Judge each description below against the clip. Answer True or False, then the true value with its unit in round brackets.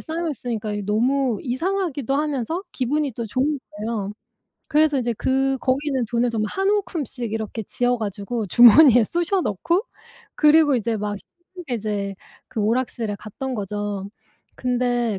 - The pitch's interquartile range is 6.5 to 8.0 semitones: False (5.3 semitones)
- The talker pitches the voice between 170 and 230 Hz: False (245 Hz)